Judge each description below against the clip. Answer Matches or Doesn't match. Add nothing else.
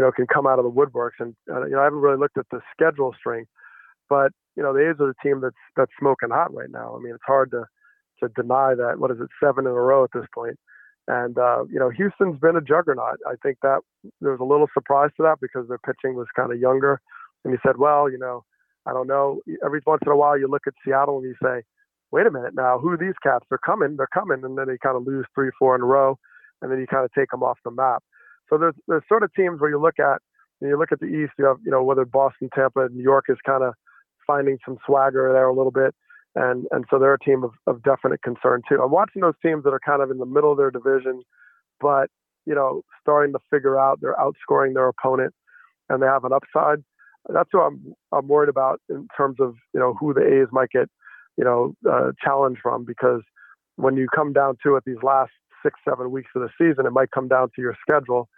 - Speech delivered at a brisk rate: Matches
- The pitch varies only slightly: Matches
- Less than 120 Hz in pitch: Doesn't match